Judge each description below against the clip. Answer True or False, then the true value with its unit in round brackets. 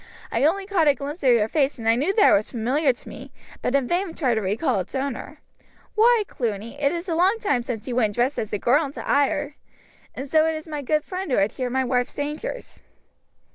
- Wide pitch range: False (4.9 semitones)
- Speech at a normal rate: False (235 wpm)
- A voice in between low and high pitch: False (280 Hz)